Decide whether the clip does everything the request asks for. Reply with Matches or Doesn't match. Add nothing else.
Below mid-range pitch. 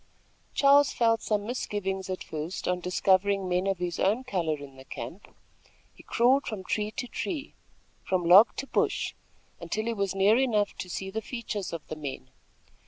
Doesn't match